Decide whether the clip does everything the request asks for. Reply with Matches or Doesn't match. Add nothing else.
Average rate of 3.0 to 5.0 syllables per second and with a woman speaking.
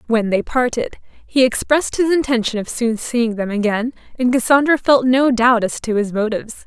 Doesn't match